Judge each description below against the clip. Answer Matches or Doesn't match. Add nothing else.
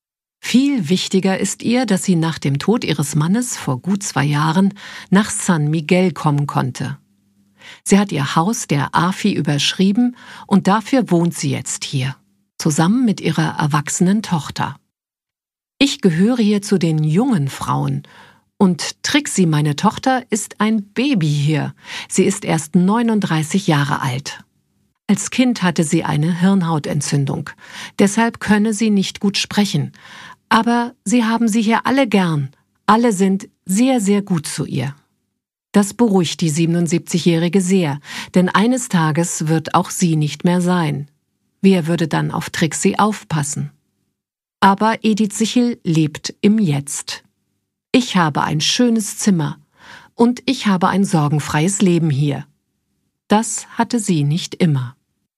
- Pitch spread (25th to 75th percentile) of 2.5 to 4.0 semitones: Doesn't match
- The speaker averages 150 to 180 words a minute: Doesn't match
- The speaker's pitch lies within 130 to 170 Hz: Doesn't match